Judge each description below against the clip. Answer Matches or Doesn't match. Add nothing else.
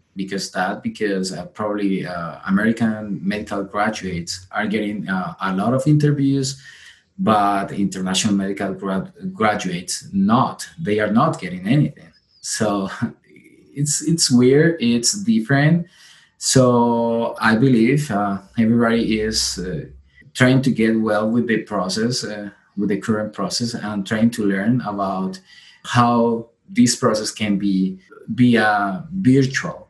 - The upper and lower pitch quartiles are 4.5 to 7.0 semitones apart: Doesn't match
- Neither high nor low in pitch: Doesn't match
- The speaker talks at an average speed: Doesn't match